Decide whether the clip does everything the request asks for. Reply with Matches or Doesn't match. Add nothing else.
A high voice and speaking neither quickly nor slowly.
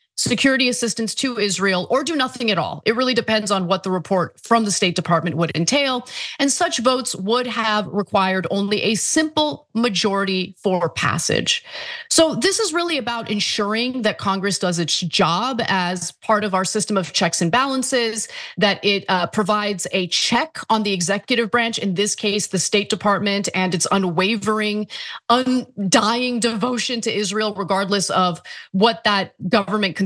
Matches